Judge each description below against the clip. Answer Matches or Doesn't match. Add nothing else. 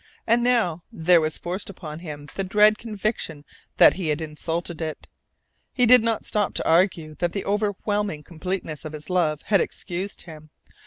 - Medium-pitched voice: Matches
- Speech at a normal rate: Matches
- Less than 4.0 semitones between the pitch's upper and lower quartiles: Doesn't match